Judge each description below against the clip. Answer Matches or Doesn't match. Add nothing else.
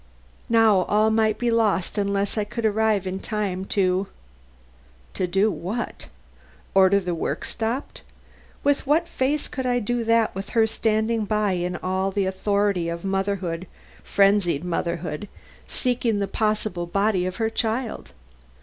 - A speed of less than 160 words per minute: Matches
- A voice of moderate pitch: Doesn't match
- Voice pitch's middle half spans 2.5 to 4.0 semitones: Matches